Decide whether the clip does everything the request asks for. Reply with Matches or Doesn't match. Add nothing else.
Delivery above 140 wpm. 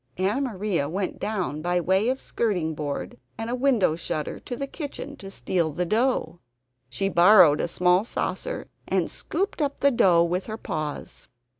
Matches